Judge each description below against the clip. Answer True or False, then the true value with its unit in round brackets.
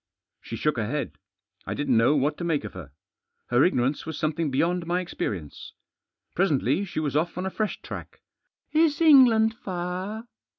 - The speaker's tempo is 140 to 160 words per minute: False (170 wpm)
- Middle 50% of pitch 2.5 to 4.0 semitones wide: False (5.5 semitones)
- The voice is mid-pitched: True (165 Hz)